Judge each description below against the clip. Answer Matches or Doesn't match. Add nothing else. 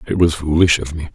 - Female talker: Doesn't match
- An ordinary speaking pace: Doesn't match